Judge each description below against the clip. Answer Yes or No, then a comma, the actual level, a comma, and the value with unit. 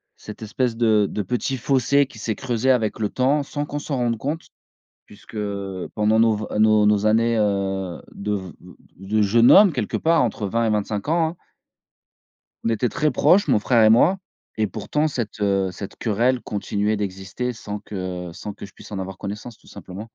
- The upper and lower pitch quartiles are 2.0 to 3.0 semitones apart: No, average, 3.5 semitones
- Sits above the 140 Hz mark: No, low, 110 Hz